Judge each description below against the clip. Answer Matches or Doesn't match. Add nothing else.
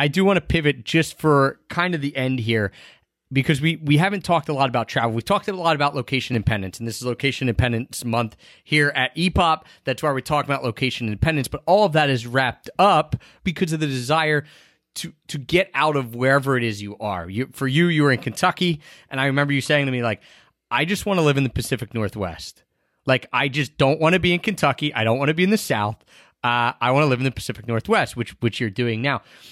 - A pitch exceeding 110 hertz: Matches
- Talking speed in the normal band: Doesn't match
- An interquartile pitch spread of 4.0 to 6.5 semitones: Matches